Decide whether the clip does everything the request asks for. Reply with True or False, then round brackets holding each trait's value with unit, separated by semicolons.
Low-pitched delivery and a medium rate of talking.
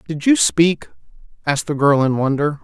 False (150 Hz; 180 wpm)